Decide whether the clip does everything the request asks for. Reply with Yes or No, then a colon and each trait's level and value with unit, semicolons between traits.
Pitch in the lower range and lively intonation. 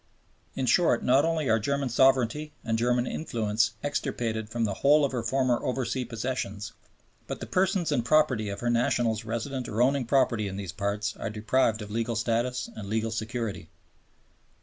No: low, 120 Hz; average, 3.1 semitones